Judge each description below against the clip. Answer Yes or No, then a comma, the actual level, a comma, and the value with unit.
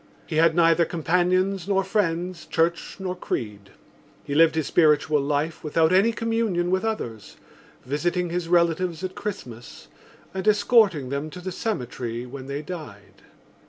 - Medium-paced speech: Yes, average, 145 wpm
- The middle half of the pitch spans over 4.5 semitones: No, average, 4.1 semitones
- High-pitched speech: No, medium, 170 Hz